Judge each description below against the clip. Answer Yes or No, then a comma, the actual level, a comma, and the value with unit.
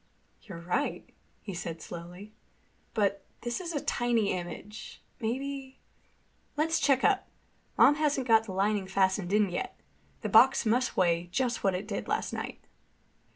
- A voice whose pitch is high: Yes, high, 215 Hz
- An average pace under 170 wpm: Yes, average, 150 wpm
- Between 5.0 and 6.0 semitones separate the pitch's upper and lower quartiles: Yes, wide, 5.5 semitones